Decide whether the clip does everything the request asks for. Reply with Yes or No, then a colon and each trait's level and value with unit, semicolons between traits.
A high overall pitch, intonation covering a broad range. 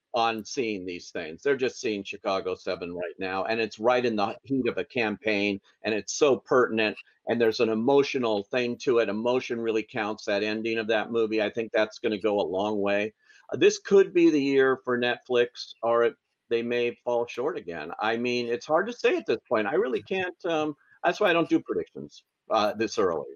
No: low, 120 Hz; wide, 6.6 semitones